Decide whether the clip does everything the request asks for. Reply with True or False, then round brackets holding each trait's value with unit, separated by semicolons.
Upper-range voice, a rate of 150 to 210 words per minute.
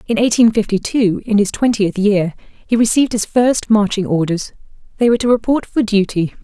True (215 Hz; 185 wpm)